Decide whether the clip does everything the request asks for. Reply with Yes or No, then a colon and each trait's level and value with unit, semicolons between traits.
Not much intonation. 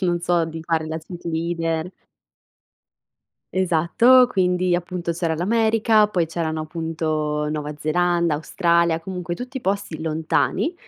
Yes: narrow, 2.2 semitones